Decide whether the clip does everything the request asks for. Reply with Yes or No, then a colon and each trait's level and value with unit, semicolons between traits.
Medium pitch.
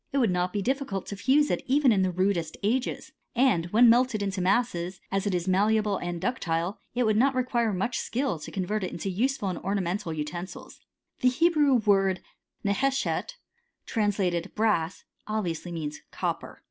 No: high, 200 Hz